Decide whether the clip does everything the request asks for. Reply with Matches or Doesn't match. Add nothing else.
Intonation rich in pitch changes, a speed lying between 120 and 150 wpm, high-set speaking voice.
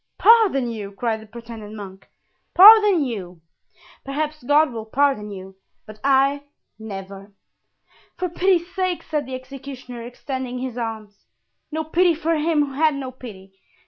Matches